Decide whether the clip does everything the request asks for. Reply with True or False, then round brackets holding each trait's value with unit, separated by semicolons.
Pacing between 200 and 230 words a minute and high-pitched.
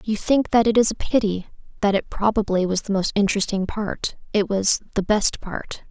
True (205 wpm; 205 Hz)